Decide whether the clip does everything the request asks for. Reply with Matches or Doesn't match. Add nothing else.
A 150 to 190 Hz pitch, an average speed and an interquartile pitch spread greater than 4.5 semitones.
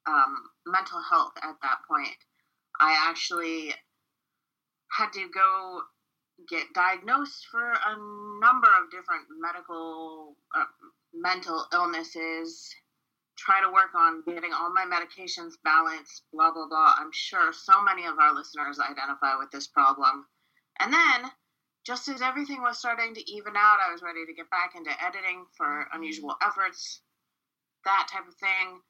Matches